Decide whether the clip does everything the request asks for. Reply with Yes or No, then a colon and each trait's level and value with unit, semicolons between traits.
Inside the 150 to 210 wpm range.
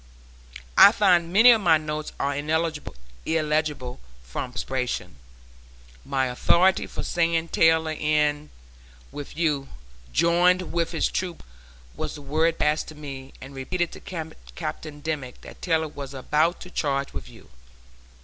No: average, 140 wpm